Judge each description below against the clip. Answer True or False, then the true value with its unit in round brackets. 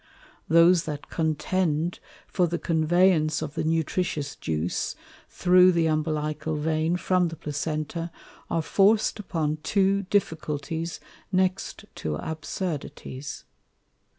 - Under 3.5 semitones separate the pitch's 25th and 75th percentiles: True (2.8 semitones)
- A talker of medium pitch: True (160 Hz)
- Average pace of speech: False (105 wpm)